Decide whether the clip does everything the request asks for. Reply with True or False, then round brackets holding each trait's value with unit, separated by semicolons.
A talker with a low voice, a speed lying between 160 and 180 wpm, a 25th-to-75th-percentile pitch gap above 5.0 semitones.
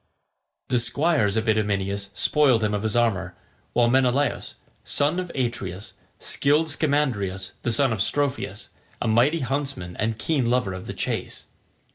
False (120 Hz; 145 wpm; 5.5 semitones)